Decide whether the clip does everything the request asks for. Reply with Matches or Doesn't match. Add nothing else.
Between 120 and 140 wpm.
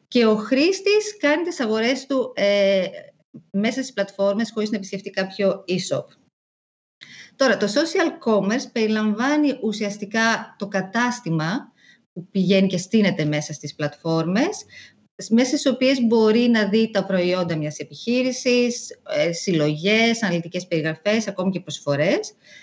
Matches